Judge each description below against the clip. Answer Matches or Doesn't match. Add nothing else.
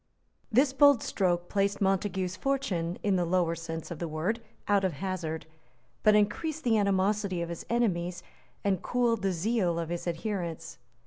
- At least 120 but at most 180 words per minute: Matches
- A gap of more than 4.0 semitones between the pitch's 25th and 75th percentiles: Doesn't match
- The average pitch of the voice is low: Doesn't match